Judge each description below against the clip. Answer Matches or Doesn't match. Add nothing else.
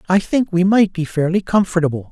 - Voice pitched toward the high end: Doesn't match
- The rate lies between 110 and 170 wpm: Doesn't match